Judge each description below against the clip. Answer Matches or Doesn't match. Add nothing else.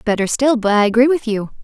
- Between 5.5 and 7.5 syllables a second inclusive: Matches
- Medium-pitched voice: Doesn't match